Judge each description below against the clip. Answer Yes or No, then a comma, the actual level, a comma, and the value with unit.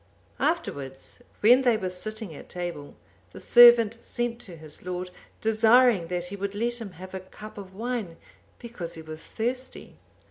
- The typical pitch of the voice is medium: No, high, 205 Hz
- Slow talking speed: No, average, 165 wpm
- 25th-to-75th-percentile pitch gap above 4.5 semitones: Yes, average, 4.9 semitones